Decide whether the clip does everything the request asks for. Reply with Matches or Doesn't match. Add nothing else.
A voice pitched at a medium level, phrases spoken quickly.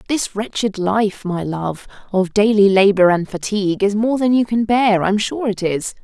Doesn't match